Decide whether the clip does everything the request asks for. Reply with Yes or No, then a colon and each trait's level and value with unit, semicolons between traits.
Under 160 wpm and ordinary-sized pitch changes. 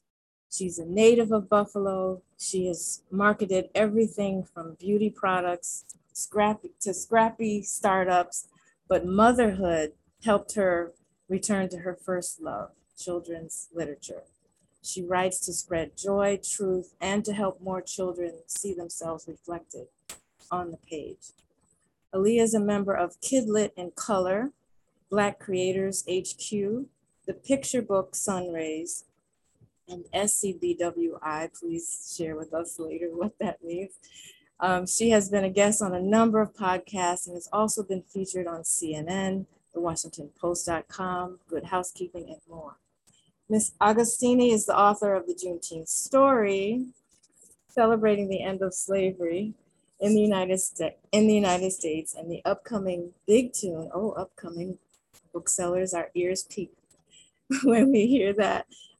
Yes: average, 140 wpm; average, 3.0 semitones